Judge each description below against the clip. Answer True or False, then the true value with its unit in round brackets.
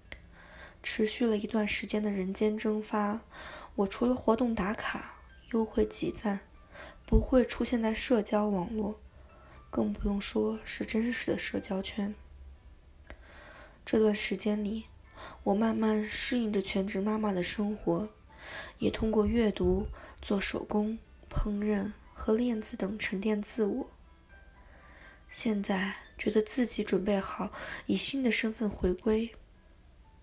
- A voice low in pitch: False (210 Hz)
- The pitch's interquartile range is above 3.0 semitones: False (2.5 semitones)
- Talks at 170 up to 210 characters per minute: True (190 characters per minute)